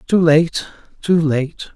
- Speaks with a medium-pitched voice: Yes, medium, 160 Hz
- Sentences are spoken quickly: No, slow, 105 wpm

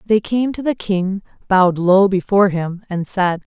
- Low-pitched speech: No, high, 195 Hz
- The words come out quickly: No, average, 185 wpm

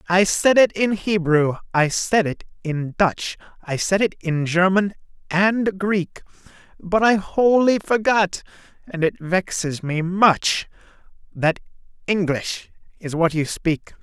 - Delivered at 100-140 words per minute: Yes, slow, 135 wpm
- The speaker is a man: Yes, male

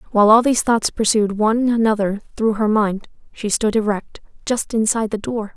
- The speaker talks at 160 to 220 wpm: Yes, average, 185 wpm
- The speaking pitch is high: Yes, high, 215 Hz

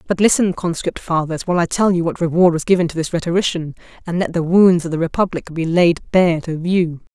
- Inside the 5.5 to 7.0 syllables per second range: Yes, 5.8 syllables/s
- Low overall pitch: No, medium, 170 Hz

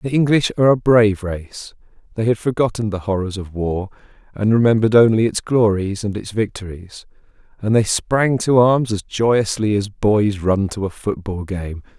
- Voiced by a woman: No, male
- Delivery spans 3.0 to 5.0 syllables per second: Yes, 4.8 syllables/s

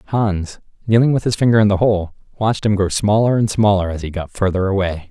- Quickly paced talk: Yes, fast, 225 wpm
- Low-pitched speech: Yes, low, 100 Hz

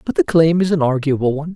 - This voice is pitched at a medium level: Yes, medium, 150 Hz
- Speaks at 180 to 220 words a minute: No, fast, 270 wpm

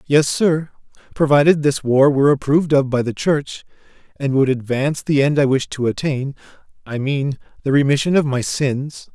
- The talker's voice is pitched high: No, medium, 140 Hz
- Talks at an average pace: Yes, average, 170 wpm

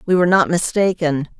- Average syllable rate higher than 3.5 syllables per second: Yes, 6.0 syllables/s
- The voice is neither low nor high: Yes, medium, 170 Hz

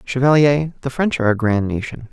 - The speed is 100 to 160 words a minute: No, average, 200 wpm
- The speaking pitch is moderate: No, low, 130 Hz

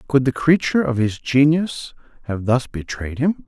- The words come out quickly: No, average, 175 wpm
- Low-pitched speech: Yes, low, 130 Hz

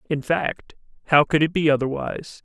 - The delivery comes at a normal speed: Yes, average, 170 wpm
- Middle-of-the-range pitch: Yes, medium, 150 Hz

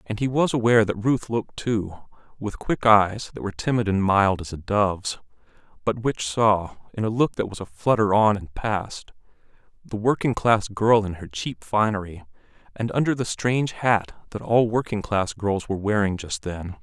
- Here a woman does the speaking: No, male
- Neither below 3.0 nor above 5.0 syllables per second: Yes, 4.9 syllables/s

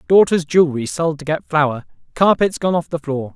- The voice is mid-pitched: Yes, medium, 160 Hz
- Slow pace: No, average, 195 wpm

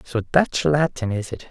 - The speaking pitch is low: Yes, low, 130 Hz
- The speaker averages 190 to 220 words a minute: Yes, average, 200 wpm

